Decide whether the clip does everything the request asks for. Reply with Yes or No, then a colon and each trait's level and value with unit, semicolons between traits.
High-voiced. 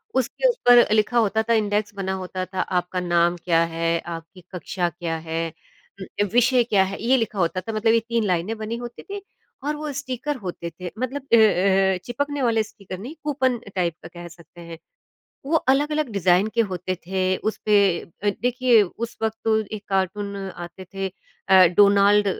Yes: high, 205 Hz